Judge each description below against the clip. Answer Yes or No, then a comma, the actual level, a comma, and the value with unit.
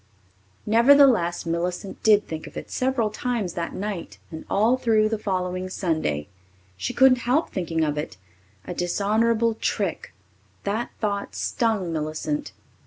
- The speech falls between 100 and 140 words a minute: Yes, slow, 135 wpm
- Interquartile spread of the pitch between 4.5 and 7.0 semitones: Yes, average, 5.2 semitones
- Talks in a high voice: Yes, high, 200 Hz